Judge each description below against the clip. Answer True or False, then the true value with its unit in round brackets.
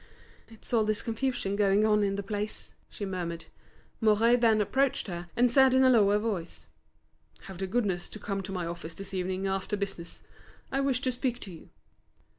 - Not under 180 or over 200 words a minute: True (190 wpm)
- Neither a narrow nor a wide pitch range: True (3.3 semitones)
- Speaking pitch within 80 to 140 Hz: False (205 Hz)